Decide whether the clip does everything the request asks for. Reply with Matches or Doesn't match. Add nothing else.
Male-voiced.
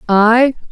Doesn't match